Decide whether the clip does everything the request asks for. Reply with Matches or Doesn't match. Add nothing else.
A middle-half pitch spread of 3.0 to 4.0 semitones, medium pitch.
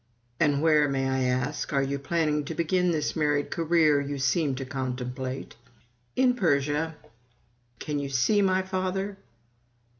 Matches